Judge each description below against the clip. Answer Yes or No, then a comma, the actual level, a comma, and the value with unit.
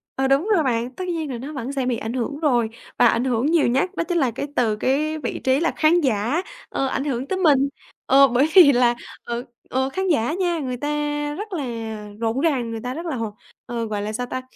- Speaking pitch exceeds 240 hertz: Yes, very high, 270 Hz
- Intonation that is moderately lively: Yes, average, 4.3 semitones